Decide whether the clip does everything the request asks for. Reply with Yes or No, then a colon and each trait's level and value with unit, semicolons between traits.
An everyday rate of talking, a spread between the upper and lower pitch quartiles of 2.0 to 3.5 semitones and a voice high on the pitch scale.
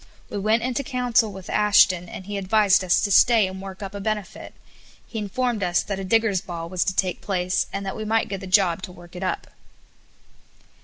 No: fast, 215 wpm; average, 2.7 semitones; high, 195 Hz